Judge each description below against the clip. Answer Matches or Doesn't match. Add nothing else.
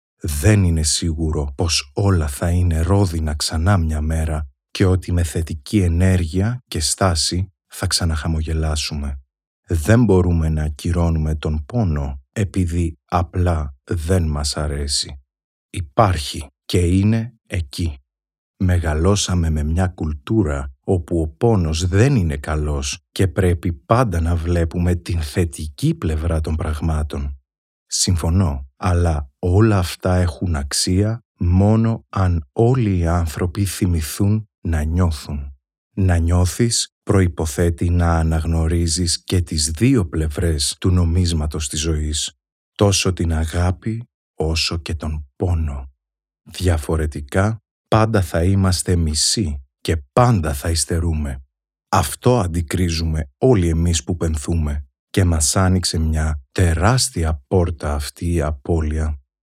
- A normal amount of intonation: Matches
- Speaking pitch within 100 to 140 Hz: Doesn't match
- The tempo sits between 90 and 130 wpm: Matches